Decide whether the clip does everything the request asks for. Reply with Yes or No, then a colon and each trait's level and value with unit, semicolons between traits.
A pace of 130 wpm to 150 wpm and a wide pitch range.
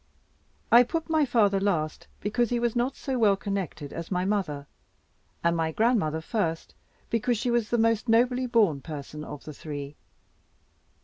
No: average, 165 wpm; wide, 6.9 semitones